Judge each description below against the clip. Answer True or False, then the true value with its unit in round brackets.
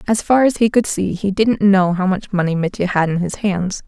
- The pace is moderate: False (265 wpm)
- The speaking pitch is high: True (195 Hz)